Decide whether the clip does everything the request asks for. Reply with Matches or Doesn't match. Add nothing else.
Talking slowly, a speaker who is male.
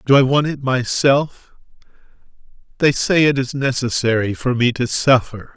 Doesn't match